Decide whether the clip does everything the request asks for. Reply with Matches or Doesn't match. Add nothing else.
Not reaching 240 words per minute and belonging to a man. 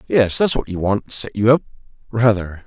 Matches